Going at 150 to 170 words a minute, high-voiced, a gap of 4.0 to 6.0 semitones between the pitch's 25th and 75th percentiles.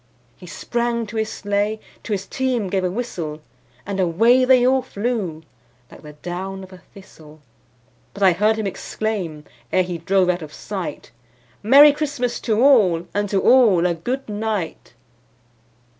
Yes: average, 160 wpm; high, 200 Hz; average, 4.7 semitones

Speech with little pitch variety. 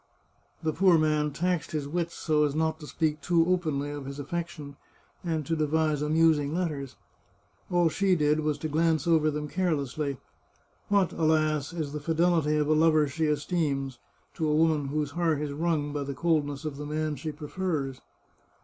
Yes: narrow, 2.0 semitones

